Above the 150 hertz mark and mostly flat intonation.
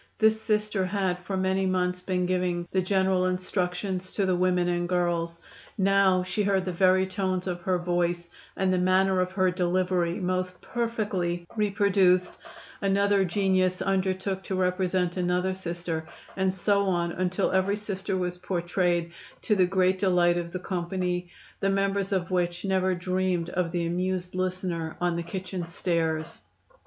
Yes: medium, 185 Hz; narrow, 1.3 semitones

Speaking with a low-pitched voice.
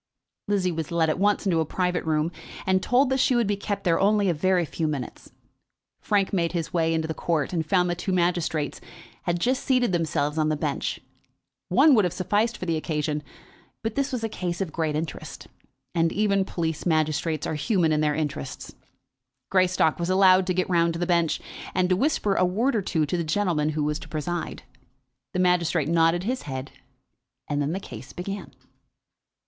No: medium, 175 Hz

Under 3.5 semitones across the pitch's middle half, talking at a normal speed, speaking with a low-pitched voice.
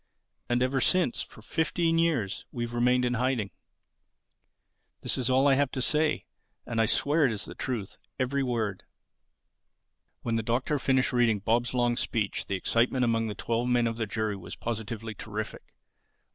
Yes: average, 2.7 semitones; average, 170 wpm; low, 120 Hz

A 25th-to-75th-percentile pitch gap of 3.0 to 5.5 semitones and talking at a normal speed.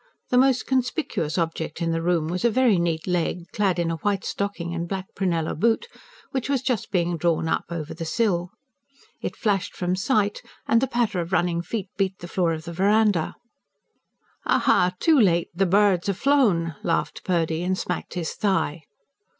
Yes: average, 3.7 semitones; average, 185 wpm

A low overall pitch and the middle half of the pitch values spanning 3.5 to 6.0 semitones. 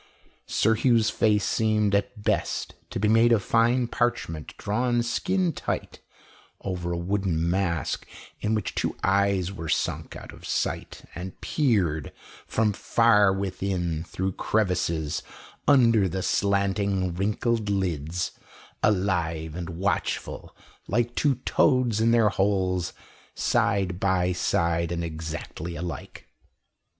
Yes: low, 100 Hz; average, 4.1 semitones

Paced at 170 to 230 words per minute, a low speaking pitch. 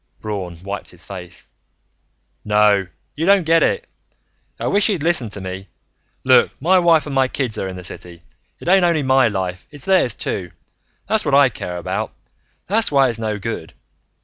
Yes: average, 180 wpm; low, 120 Hz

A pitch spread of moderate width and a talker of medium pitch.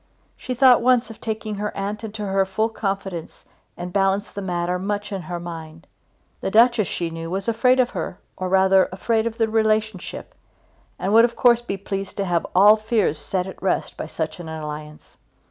No: average, 3.5 semitones; high, 195 Hz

